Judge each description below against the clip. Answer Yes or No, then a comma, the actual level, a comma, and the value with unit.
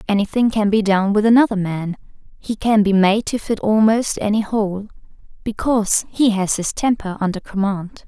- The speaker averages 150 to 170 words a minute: Yes, average, 155 wpm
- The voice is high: Yes, high, 210 Hz